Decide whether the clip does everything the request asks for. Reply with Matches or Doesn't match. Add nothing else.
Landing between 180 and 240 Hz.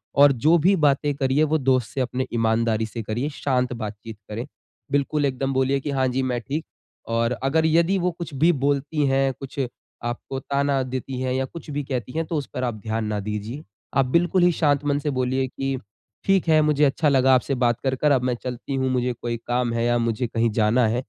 Doesn't match